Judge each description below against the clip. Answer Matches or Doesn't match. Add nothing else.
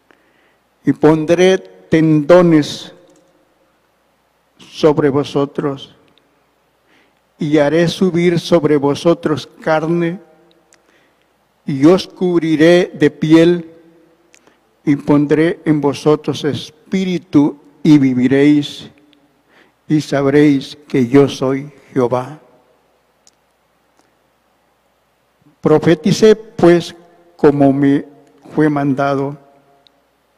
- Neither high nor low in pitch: Matches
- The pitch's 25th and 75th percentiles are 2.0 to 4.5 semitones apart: Matches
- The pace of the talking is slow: Matches